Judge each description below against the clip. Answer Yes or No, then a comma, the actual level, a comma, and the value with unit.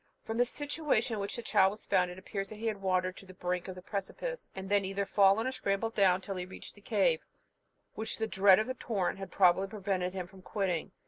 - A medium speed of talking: No, fast, 245 wpm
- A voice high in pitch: Yes, high, 195 Hz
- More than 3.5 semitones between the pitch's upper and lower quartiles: No, average, 2.7 semitones